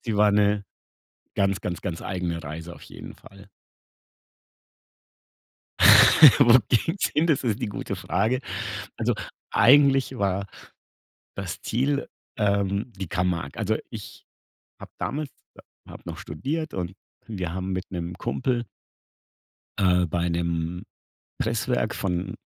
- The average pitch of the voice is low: Yes, low, 100 Hz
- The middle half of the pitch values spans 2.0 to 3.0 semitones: No, average, 4.9 semitones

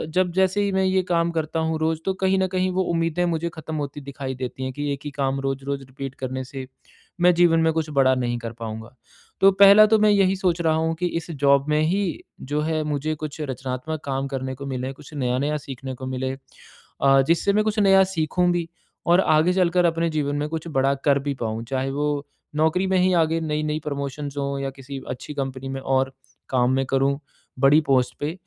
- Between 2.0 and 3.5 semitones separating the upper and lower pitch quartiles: No, average, 3.9 semitones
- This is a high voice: No, medium, 150 Hz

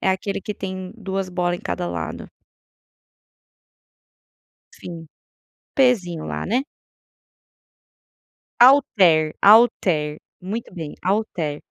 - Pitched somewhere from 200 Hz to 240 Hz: No, medium, 185 Hz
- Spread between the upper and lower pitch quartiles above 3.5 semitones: Yes, average, 4.3 semitones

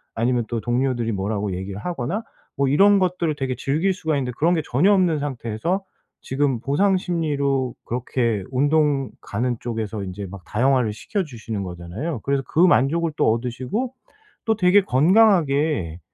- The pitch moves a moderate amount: No, wide, 6.3 semitones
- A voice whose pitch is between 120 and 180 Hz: Yes, low, 135 Hz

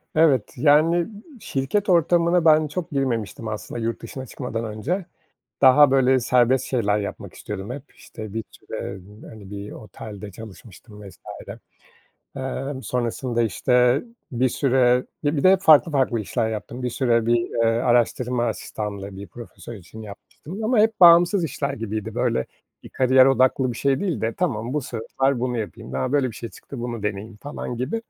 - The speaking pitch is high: No, low, 125 Hz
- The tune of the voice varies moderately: Yes, average, 4.4 semitones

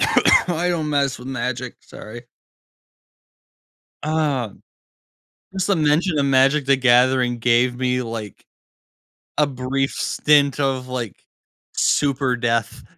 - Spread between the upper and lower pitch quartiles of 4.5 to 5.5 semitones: No, average, 3.0 semitones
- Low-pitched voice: Yes, low, 130 Hz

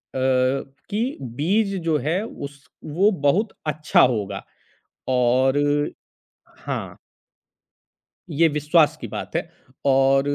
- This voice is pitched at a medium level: Yes, medium, 145 Hz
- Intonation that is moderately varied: Yes, average, 4.1 semitones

